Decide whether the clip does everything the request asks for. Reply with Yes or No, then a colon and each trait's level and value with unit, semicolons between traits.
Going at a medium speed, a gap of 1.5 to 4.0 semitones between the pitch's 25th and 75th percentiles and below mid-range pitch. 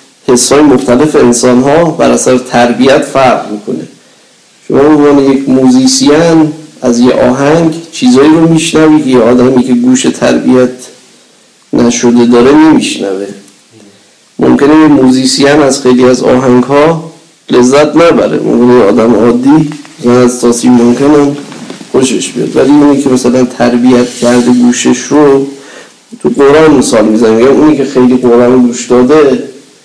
Yes: average, 125 wpm; average, 3.1 semitones; low, 130 Hz